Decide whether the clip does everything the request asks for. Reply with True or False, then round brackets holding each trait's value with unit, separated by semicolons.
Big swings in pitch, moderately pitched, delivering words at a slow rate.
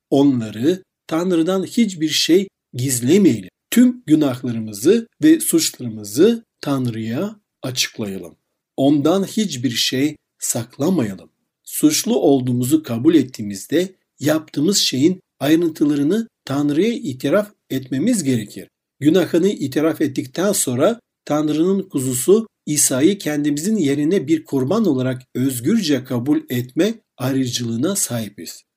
True (7.4 semitones; 150 Hz; 90 wpm)